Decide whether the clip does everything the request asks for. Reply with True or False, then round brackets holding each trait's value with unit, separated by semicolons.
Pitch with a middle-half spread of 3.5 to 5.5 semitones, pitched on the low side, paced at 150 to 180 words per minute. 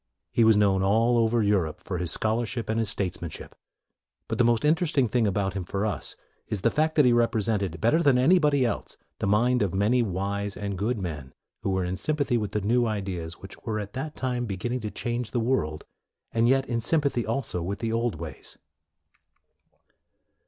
False (3.8 semitones; 110 Hz; 200 wpm)